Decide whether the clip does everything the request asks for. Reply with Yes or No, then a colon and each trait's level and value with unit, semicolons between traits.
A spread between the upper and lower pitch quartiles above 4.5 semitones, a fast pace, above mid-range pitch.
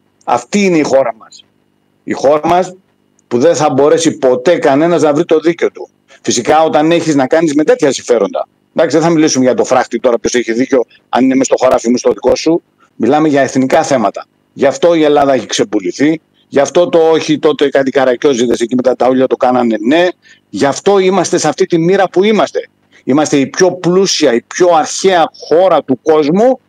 No: average, 5.2 semitones; fast, 200 wpm; medium, 155 Hz